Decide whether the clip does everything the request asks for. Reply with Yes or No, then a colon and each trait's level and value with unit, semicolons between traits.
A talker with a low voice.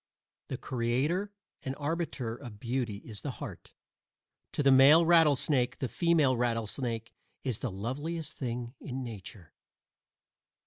Yes: low, 130 Hz